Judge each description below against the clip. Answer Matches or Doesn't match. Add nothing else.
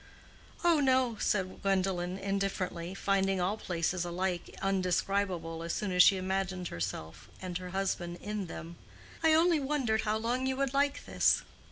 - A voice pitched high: Matches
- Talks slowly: Doesn't match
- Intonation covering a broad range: Doesn't match